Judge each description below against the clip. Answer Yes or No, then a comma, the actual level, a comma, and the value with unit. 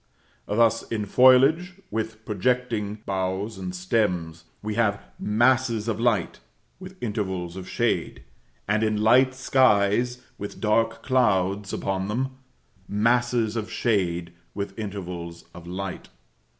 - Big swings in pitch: No, average, 3.8 semitones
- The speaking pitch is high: No, low, 105 Hz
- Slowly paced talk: Yes, slow, 120 wpm